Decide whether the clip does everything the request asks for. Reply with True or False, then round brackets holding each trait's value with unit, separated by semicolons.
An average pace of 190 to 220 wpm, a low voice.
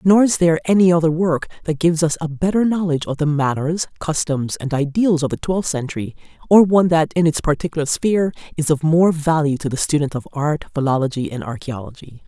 False (200 wpm; 160 Hz)